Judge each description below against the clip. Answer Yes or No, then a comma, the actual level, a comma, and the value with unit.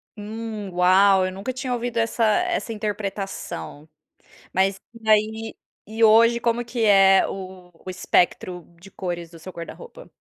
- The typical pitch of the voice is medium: No, high, 205 Hz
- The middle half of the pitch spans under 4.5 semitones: Yes, average, 3.5 semitones